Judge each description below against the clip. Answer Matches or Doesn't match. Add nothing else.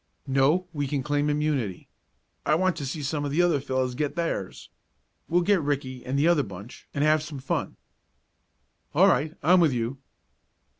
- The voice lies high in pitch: Doesn't match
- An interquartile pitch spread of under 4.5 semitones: Matches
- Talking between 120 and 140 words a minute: Doesn't match